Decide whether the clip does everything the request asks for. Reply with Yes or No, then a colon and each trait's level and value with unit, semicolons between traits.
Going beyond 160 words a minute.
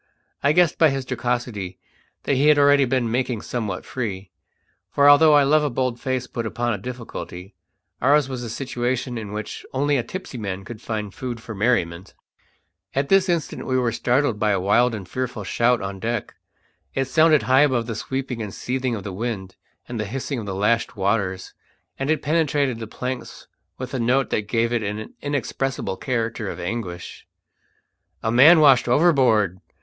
Yes: average, 185 wpm